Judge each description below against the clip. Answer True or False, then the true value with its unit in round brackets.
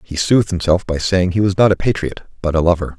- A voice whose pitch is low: True (90 Hz)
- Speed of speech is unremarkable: False (260 wpm)